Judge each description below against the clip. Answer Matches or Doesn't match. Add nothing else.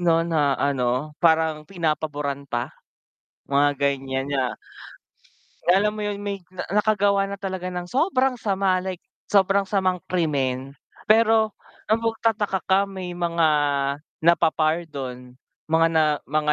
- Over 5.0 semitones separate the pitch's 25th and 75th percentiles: Matches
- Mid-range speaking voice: Matches